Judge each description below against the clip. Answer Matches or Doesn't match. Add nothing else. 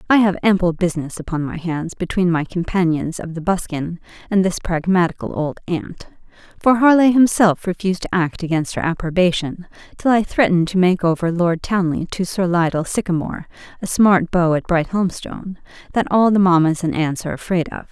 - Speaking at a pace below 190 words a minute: Matches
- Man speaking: Doesn't match